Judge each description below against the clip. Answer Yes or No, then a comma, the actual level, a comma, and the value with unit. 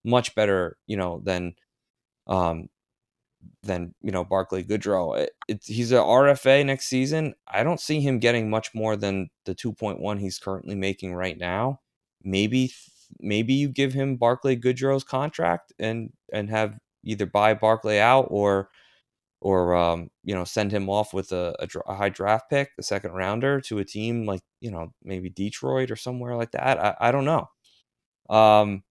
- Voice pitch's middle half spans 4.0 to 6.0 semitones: Yes, average, 4.6 semitones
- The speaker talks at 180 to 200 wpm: No, average, 170 wpm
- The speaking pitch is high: No, low, 105 Hz